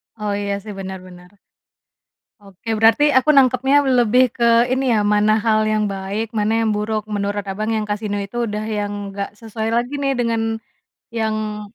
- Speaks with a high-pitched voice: Yes, high, 215 Hz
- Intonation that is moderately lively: No, narrow, 2.2 semitones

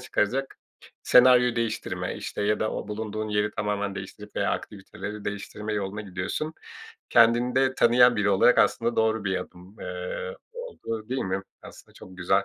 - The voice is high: No, low, 110 Hz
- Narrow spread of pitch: No, average, 3.3 semitones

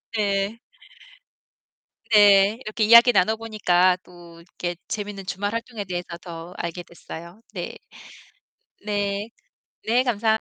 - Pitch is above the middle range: Yes, high, 200 Hz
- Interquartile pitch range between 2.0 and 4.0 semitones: Yes, average, 3.5 semitones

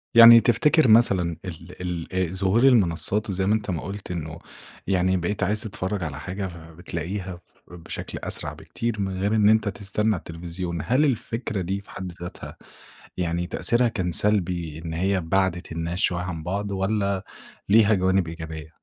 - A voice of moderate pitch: No, very low, 95 Hz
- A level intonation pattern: No, average, 3.2 semitones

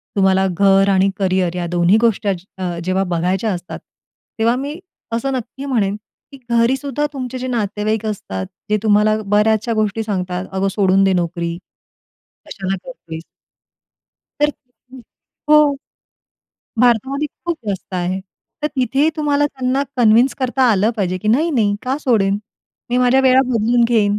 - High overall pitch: Yes, high, 215 Hz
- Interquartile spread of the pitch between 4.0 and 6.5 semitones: Yes, average, 4.9 semitones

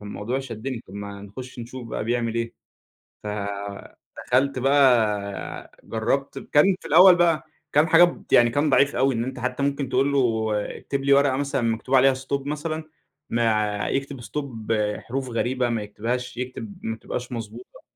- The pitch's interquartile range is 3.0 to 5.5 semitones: Yes, average, 3.6 semitones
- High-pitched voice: No, low, 125 Hz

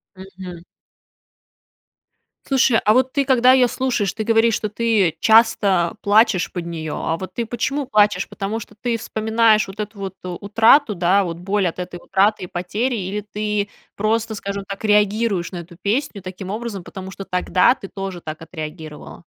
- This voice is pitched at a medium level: No, high, 205 Hz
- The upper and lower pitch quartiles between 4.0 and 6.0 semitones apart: No, average, 3.6 semitones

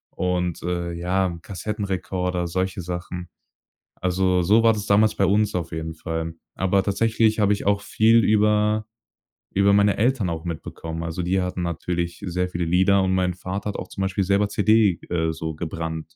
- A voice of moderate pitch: No, very low, 95 Hz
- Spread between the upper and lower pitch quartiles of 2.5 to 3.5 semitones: Yes, average, 2.8 semitones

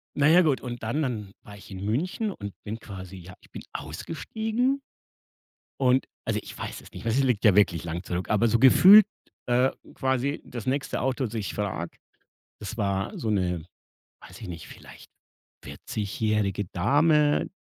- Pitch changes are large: Yes, wide, 5.9 semitones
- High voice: No, low, 115 Hz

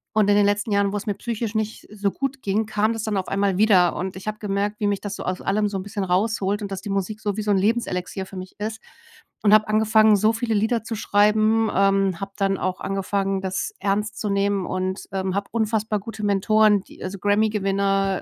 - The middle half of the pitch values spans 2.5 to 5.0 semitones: No, narrow, 1.7 semitones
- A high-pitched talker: Yes, high, 205 Hz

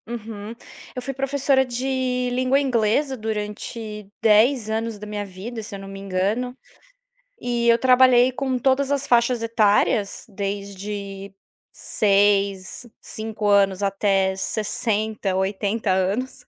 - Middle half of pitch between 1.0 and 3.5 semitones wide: No, average, 3.9 semitones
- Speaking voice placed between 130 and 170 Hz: No, high, 220 Hz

